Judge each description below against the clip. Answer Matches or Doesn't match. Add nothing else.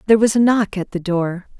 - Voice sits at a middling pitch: Doesn't match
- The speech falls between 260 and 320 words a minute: Matches